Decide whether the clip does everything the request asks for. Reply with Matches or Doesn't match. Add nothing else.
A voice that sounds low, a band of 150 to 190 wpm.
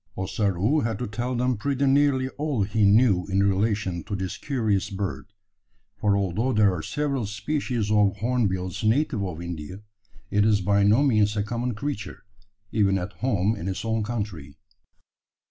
Matches